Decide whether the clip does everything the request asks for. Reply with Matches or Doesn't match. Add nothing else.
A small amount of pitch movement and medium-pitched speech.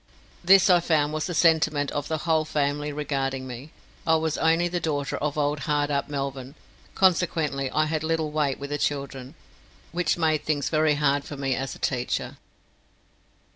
Matches